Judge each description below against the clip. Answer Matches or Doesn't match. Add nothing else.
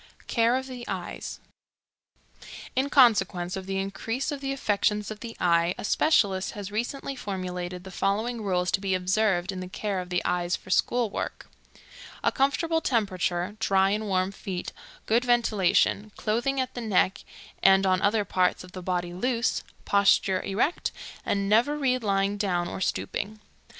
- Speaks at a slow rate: Doesn't match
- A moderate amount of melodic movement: Matches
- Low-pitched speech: Doesn't match